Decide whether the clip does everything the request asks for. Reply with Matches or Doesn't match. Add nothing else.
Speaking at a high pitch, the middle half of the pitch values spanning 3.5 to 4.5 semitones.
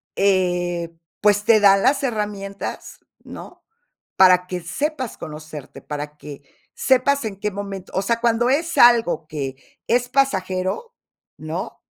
Doesn't match